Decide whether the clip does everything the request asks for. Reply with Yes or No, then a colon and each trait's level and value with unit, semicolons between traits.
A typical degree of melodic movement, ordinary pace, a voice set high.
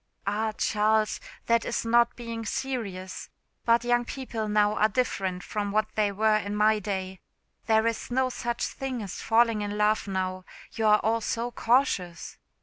No: narrow, 2.2 semitones; average, 165 wpm; high, 215 Hz